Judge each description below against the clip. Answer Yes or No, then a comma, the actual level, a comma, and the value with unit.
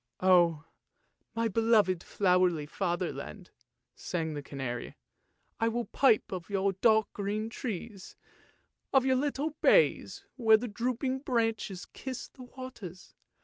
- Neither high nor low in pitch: No, high, 210 Hz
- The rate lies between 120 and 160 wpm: Yes, average, 140 wpm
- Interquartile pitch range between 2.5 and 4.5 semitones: No, average, 5.1 semitones